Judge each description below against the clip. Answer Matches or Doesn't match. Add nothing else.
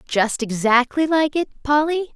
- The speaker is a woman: Matches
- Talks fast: Doesn't match